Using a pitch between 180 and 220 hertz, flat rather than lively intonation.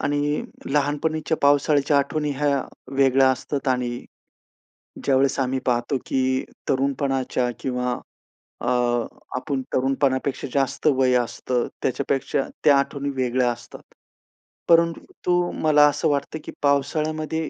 No: medium, 140 Hz; narrow, 2.1 semitones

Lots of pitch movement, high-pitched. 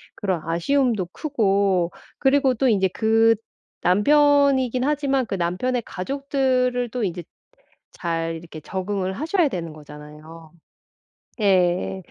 Yes: wide, 7.1 semitones; high, 205 Hz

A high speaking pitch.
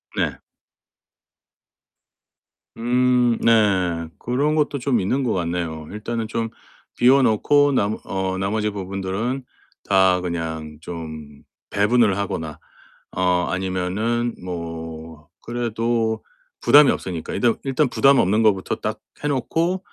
No: low, 105 Hz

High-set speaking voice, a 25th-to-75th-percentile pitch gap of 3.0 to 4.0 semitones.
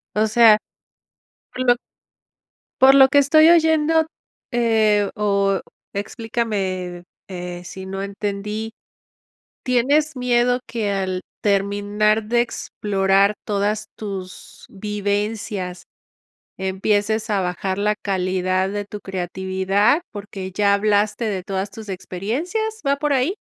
Yes: high, 205 Hz; average, 3.4 semitones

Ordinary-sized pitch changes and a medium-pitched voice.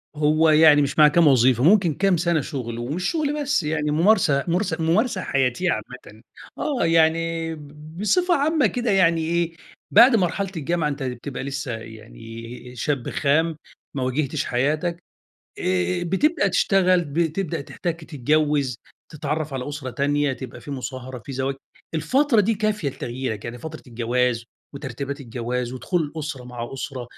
Yes: average, 4.9 semitones; medium, 150 Hz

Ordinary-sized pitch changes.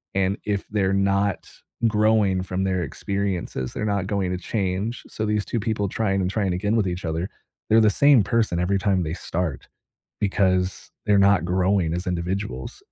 No: narrow, 2.2 semitones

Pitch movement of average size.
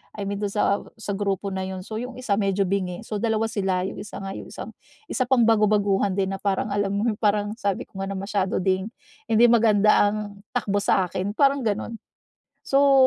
No: narrow, 2.2 semitones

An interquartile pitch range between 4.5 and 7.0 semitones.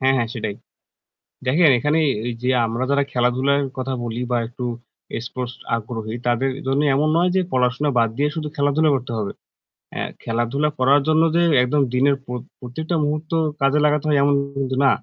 No: average, 3.2 semitones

